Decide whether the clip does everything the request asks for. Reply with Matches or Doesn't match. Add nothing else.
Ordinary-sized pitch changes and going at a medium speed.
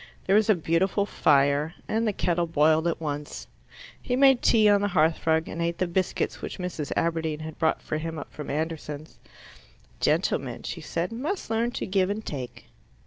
Matches